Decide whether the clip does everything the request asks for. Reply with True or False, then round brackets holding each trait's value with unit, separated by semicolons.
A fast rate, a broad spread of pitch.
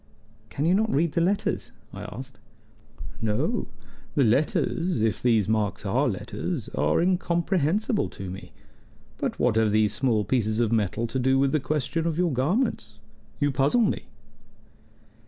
False (155 wpm; 7.2 semitones)